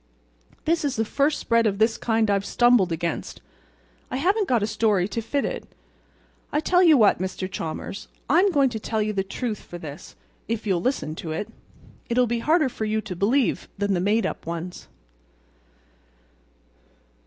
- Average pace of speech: Yes, average, 175 wpm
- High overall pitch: Yes, high, 220 Hz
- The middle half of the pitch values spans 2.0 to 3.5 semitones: No, average, 5.0 semitones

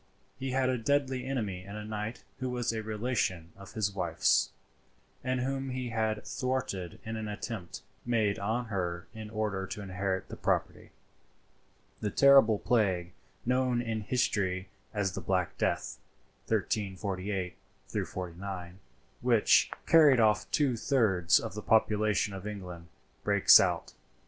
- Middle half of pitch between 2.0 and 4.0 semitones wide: No, average, 4.4 semitones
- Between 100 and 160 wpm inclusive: Yes, average, 140 wpm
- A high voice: No, low, 105 Hz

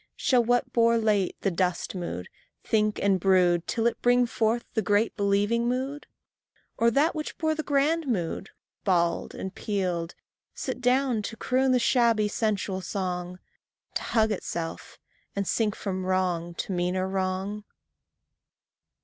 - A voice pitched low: No, high, 210 Hz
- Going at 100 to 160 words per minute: Yes, average, 145 wpm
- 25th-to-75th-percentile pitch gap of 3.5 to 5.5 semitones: Yes, average, 4.4 semitones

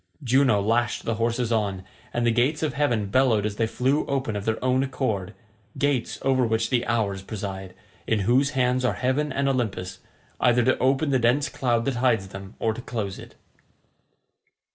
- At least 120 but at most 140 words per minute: No, average, 180 wpm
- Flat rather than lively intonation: No, average, 3.4 semitones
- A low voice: Yes, low, 120 Hz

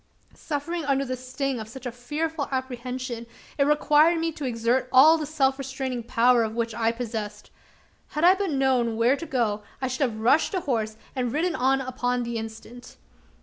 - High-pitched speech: Yes, very high, 255 Hz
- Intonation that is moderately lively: Yes, average, 3.4 semitones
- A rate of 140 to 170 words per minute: No, average, 190 wpm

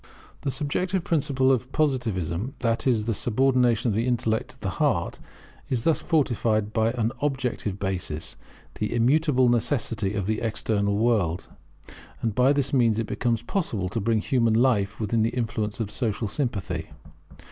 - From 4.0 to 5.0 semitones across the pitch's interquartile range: No, average, 3.5 semitones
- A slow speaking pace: No, average, 160 wpm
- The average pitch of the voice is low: Yes, low, 115 Hz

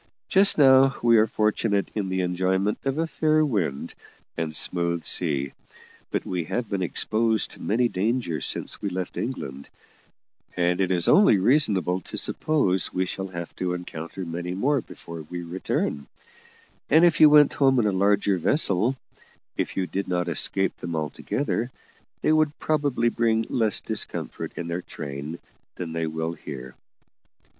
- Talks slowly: No, average, 160 wpm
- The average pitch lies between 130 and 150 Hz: No, very low, 95 Hz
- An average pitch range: No, wide, 5.9 semitones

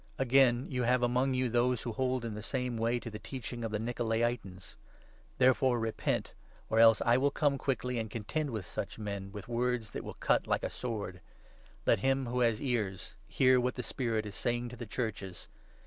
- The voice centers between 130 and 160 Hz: No, low, 120 Hz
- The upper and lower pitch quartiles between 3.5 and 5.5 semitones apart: No, narrow, 2.4 semitones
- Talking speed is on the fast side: Yes, fast, 210 wpm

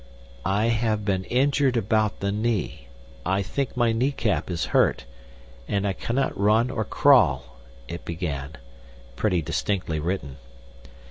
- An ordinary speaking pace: No, slow, 125 wpm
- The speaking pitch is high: No, low, 100 Hz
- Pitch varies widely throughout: Yes, wide, 6.3 semitones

